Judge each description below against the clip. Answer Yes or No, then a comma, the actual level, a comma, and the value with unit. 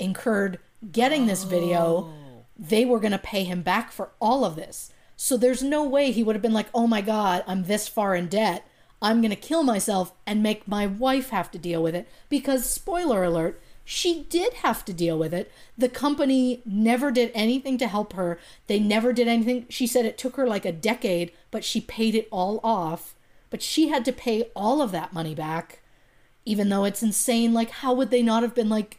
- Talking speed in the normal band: No, fast, 215 wpm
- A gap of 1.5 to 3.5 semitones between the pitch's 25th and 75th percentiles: No, average, 4.9 semitones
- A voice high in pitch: Yes, high, 220 Hz